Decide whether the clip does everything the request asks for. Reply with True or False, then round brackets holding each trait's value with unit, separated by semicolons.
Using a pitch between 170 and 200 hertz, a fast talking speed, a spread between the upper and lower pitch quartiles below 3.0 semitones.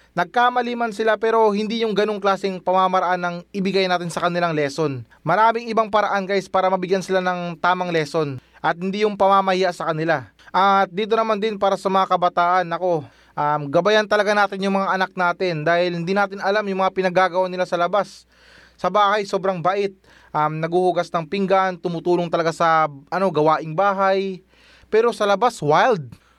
True (185 Hz; 175 wpm; 2.5 semitones)